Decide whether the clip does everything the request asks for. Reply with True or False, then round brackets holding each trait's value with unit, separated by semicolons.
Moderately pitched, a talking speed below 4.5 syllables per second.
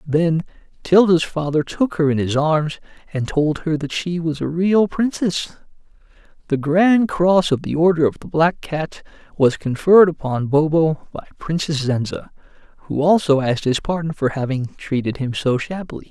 False (155 Hz; 4.7 syllables/s)